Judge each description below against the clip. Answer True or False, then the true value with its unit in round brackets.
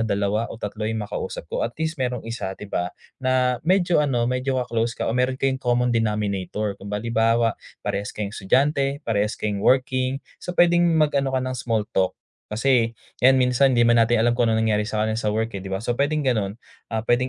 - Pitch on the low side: True (120 Hz)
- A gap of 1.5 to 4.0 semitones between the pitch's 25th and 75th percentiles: True (3.3 semitones)